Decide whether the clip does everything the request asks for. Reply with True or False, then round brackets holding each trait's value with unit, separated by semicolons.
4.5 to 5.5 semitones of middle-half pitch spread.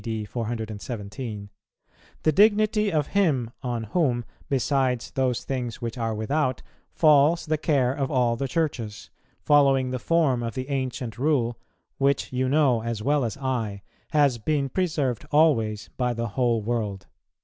False (4.1 semitones)